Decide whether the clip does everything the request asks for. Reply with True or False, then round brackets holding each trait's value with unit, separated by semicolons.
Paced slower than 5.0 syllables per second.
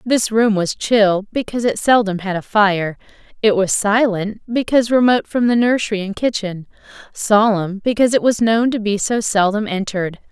False (5.2 syllables/s)